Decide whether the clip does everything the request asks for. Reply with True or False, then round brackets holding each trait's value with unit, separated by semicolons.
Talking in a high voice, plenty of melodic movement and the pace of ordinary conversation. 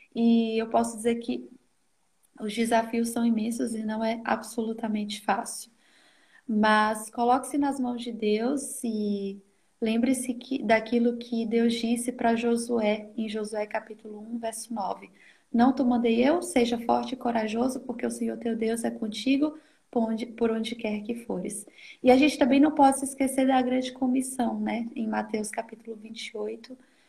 False (235 Hz; 2.4 semitones; 160 wpm)